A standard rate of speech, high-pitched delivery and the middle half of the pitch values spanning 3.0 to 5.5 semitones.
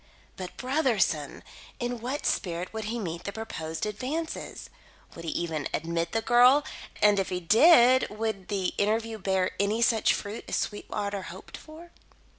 Yes: average, 155 wpm; high, 210 Hz; average, 4.7 semitones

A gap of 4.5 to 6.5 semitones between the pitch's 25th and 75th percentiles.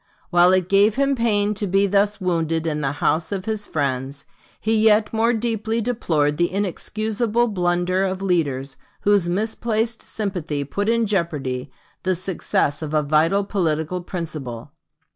Yes: average, 5.2 semitones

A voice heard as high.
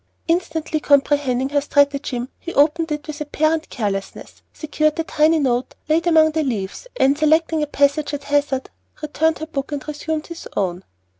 Yes: very high, 295 Hz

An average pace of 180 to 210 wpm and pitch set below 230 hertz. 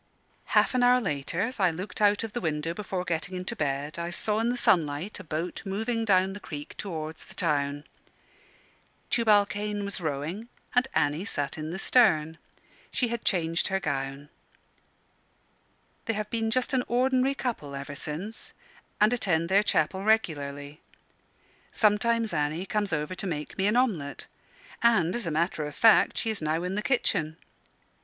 No: average, 170 wpm; medium, 185 Hz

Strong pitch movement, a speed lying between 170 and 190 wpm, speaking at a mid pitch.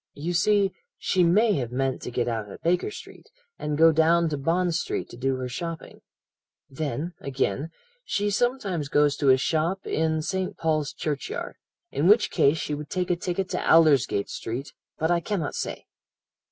No: average, 4.3 semitones; average, 180 wpm; medium, 160 Hz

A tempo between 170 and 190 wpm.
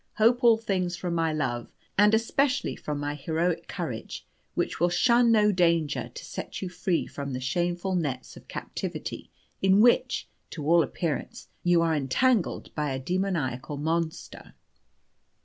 No: average, 150 wpm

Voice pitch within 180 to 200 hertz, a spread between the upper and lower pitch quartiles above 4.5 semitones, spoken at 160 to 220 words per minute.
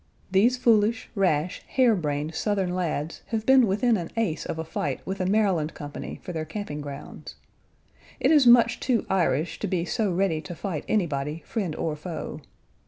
Yes: medium, 185 Hz; wide, 5.6 semitones; average, 175 wpm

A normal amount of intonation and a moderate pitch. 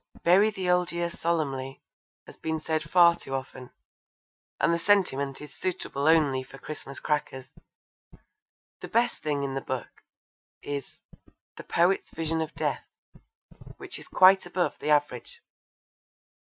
Yes: average, 4.1 semitones; medium, 155 Hz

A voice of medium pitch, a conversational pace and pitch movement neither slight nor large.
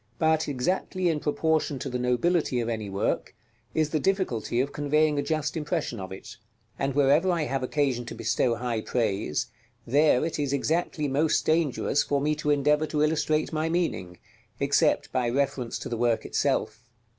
Yes: medium, 145 Hz; average, 175 wpm; average, 4.1 semitones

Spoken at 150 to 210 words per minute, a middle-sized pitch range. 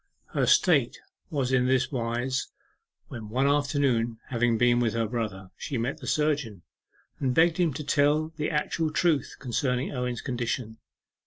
Yes: average, 155 wpm; average, 3.8 semitones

